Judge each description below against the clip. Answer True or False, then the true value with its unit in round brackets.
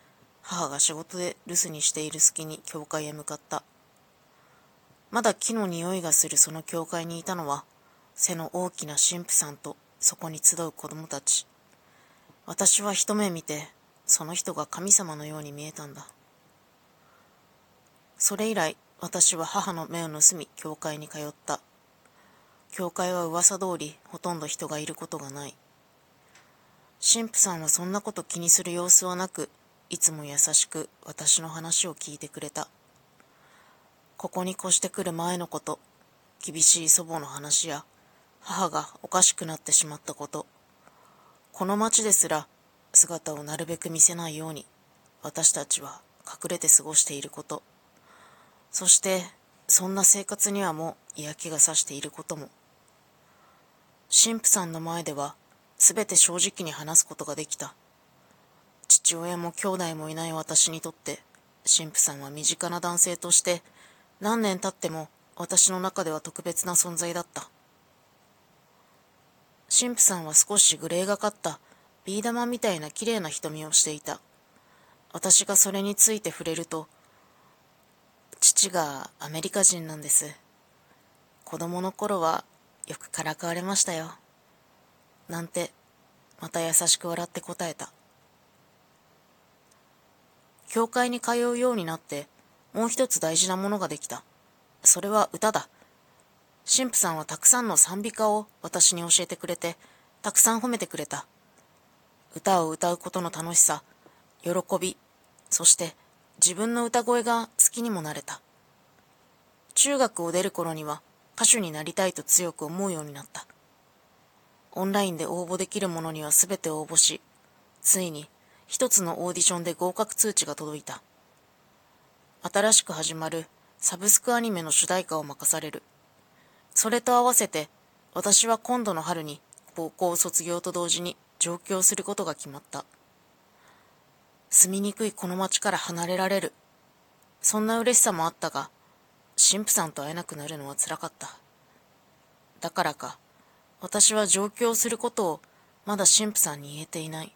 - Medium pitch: True (175 Hz)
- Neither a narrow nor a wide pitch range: True (3.7 semitones)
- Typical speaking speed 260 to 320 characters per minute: True (275 characters per minute)